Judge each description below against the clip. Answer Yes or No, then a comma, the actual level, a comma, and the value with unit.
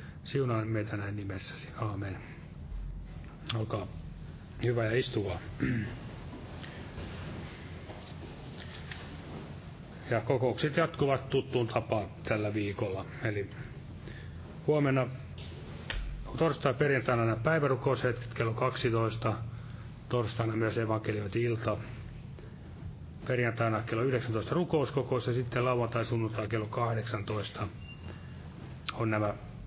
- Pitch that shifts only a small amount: No, average, 3.1 semitones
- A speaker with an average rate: No, slow, 80 wpm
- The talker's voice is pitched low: Yes, low, 115 Hz